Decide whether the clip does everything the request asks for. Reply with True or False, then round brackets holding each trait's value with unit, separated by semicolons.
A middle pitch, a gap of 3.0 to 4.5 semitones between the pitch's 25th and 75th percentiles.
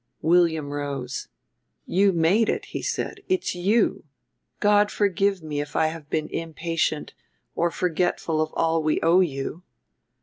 True (165 Hz; 3.3 semitones)